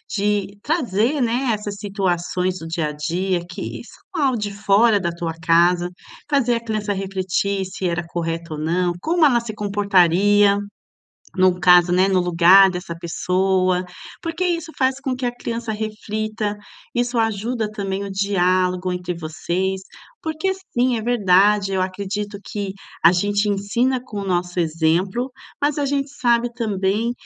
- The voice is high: Yes, high, 200 Hz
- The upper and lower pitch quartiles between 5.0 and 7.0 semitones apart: No, average, 4.2 semitones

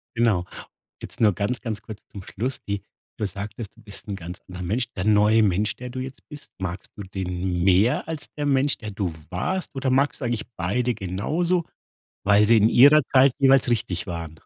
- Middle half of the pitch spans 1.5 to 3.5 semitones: No, average, 5.1 semitones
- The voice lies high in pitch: No, low, 105 Hz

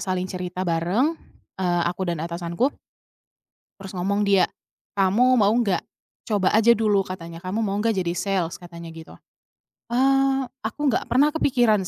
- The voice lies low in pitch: No, high, 195 Hz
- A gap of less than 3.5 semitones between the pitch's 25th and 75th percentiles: No, average, 4.4 semitones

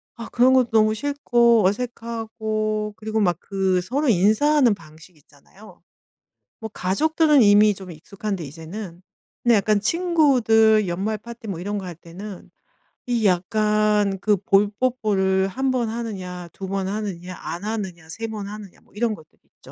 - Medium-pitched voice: No, high, 210 Hz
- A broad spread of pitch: No, average, 3.3 semitones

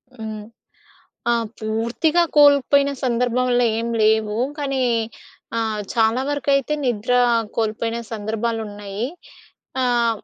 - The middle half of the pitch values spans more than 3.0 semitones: No, average, 2.7 semitones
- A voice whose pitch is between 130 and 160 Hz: No, high, 230 Hz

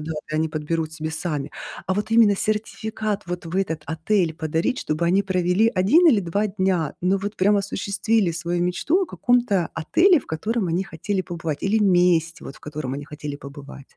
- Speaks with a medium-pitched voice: Yes, medium, 180 Hz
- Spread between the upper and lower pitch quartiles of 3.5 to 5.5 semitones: Yes, average, 4.5 semitones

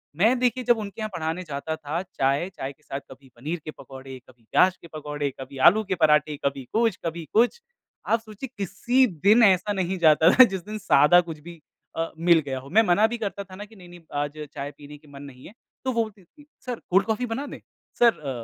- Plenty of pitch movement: Yes, wide, 6.5 semitones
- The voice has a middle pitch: Yes, medium, 175 Hz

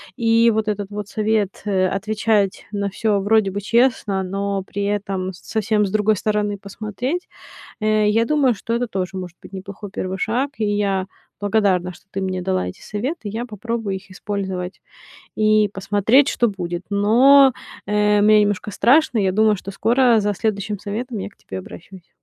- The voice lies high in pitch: Yes, high, 205 Hz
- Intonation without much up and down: Yes, narrow, 2.2 semitones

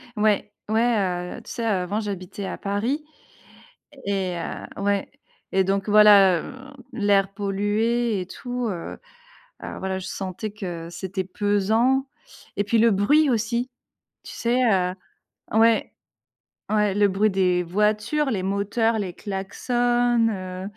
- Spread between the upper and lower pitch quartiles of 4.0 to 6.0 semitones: No, average, 2.9 semitones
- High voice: Yes, high, 205 Hz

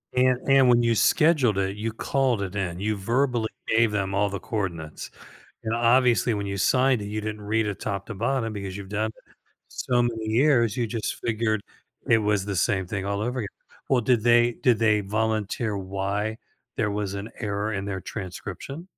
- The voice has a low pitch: Yes, low, 110 Hz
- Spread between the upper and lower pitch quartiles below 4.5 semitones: Yes, average, 2.9 semitones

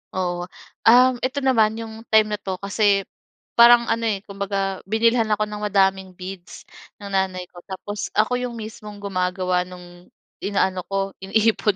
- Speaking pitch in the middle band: No, high, 200 Hz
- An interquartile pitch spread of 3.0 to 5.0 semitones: No, narrow, 2.6 semitones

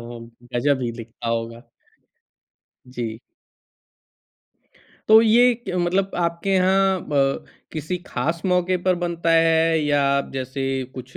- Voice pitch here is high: No, medium, 160 Hz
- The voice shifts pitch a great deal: Yes, wide, 5.9 semitones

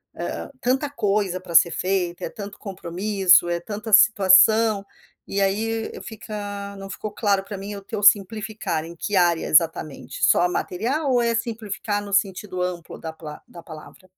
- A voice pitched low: No, high, 200 Hz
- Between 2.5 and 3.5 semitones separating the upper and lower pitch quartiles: Yes, average, 3.1 semitones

